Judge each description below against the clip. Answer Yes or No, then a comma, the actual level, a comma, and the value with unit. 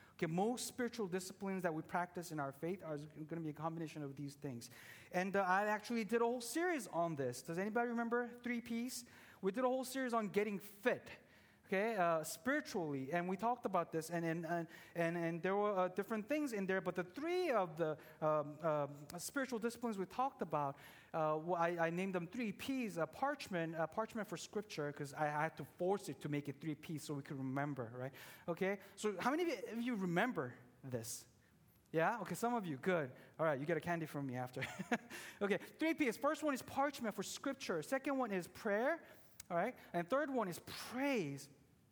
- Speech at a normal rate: No, fast, 210 wpm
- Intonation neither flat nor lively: No, wide, 7.0 semitones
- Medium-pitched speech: Yes, medium, 180 Hz